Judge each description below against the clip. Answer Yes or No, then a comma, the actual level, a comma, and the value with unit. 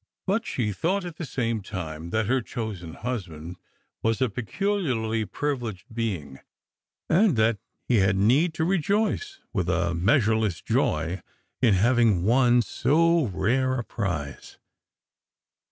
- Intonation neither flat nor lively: No, wide, 6.6 semitones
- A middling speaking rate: No, slow, 130 wpm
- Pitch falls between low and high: No, low, 115 Hz